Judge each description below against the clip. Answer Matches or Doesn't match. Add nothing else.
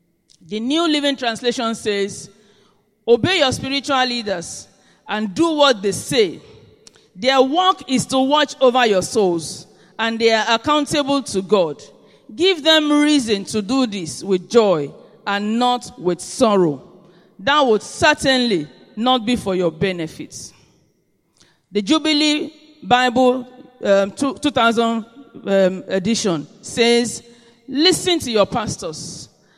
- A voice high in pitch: Matches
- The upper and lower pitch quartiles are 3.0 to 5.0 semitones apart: Doesn't match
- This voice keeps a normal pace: Doesn't match